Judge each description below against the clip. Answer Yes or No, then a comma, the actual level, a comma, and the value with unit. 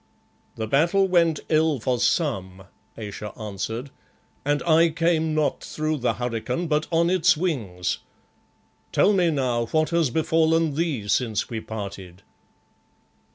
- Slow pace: Yes, slow, 130 wpm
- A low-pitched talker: No, medium, 150 Hz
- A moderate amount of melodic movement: No, wide, 6.4 semitones